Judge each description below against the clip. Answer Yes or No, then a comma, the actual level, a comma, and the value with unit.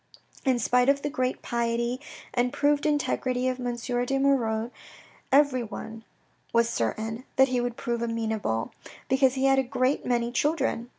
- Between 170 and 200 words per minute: No, average, 155 wpm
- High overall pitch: Yes, very high, 250 Hz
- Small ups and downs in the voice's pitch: Yes, narrow, 2.3 semitones